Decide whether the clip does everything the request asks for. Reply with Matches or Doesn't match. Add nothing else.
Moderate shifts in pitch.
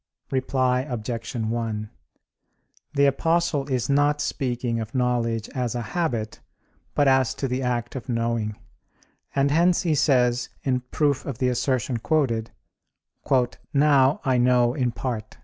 Matches